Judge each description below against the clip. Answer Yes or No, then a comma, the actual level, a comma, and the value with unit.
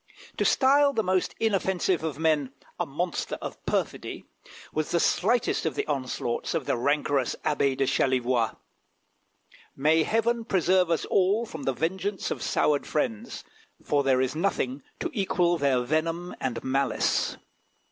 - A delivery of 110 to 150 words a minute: Yes, average, 145 wpm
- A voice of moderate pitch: Yes, medium, 160 Hz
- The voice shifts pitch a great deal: Yes, wide, 5.8 semitones